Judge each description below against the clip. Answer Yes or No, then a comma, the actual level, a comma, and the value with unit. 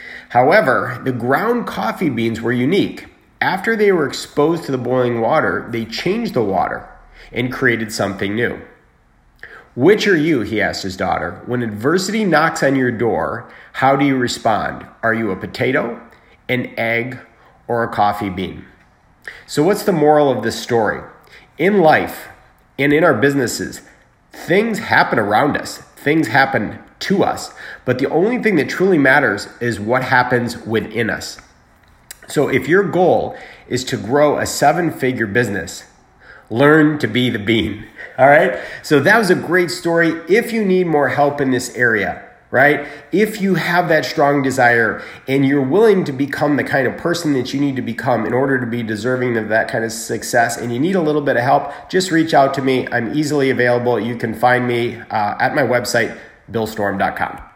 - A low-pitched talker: Yes, low, 130 Hz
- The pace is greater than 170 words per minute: Yes, average, 180 wpm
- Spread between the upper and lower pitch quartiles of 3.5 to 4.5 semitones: Yes, average, 4.1 semitones